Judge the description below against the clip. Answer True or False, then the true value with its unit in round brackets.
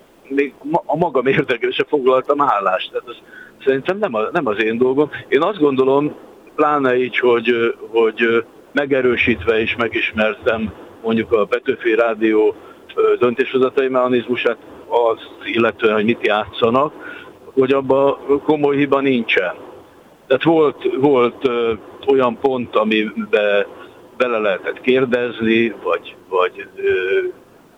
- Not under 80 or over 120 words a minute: True (110 wpm)